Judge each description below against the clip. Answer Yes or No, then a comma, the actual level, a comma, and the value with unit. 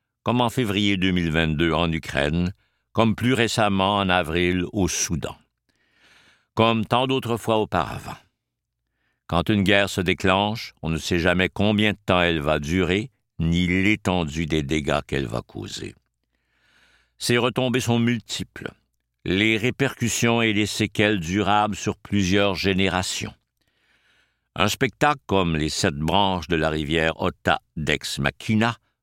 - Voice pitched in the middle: No, low, 100 Hz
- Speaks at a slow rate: Yes, slow, 135 wpm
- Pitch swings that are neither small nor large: Yes, average, 4.4 semitones